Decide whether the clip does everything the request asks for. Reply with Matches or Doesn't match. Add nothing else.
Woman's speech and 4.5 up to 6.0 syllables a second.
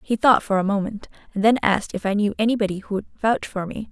Doesn't match